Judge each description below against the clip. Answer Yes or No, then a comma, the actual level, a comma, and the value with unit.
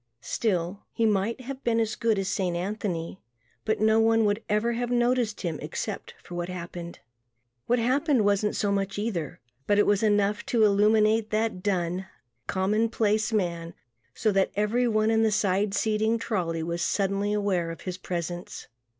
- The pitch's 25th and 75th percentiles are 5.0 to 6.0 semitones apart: No, average, 3.2 semitones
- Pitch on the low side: No, high, 205 Hz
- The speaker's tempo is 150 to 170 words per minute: Yes, average, 165 wpm